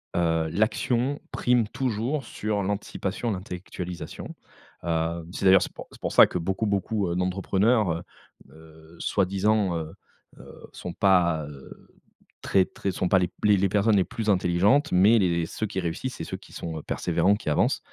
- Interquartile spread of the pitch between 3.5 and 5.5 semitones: Yes, average, 3.8 semitones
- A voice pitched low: Yes, very low, 95 Hz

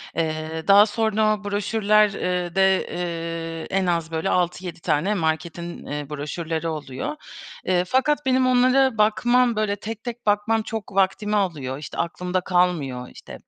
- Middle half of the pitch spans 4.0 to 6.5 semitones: Yes, average, 4.5 semitones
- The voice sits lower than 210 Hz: Yes, medium, 185 Hz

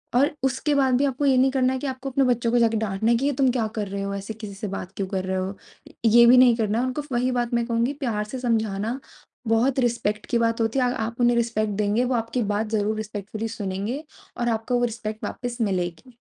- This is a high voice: Yes, high, 230 Hz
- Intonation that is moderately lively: Yes, average, 3.0 semitones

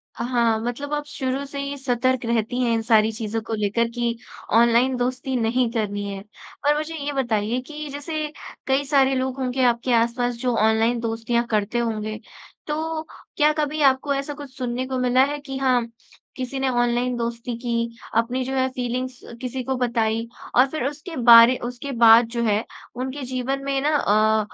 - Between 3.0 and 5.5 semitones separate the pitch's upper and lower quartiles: No, narrow, 2.5 semitones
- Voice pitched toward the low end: No, very high, 250 Hz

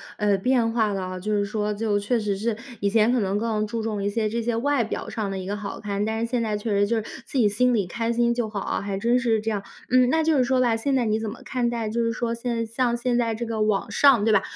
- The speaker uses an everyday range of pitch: No, narrow, 2.3 semitones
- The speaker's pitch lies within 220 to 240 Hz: Yes, high, 225 Hz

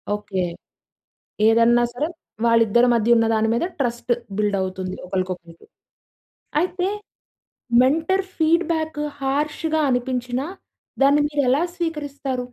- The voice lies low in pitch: No, very high, 250 Hz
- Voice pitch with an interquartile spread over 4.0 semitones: Yes, average, 5.2 semitones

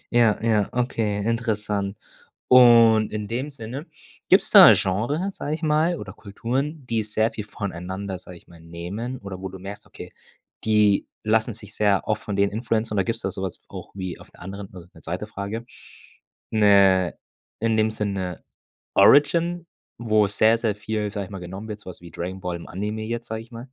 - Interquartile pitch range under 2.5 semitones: No, average, 2.9 semitones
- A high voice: No, low, 105 Hz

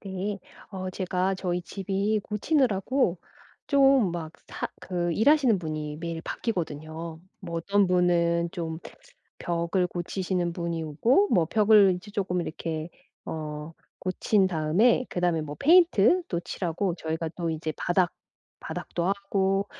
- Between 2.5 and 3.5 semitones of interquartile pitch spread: Yes, average, 3.2 semitones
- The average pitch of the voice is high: No, medium, 180 Hz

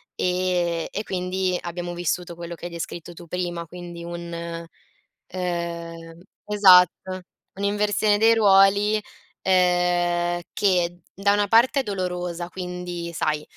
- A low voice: No, medium, 180 Hz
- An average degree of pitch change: No, narrow, 1.8 semitones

